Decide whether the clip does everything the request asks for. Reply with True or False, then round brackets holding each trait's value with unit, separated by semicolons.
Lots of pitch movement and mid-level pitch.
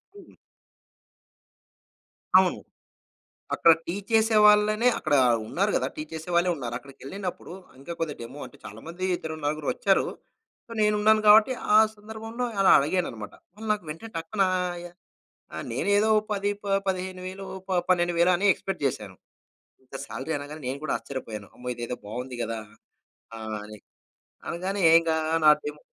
True (6.9 semitones; 175 Hz)